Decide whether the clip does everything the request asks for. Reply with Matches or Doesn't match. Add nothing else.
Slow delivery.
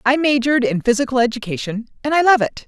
Doesn't match